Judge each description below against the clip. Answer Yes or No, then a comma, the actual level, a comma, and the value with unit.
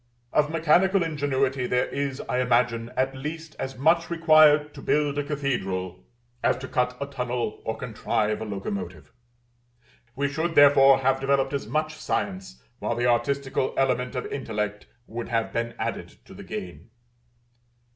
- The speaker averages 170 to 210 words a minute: No, average, 155 wpm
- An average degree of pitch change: Yes, average, 3.8 semitones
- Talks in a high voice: No, low, 130 Hz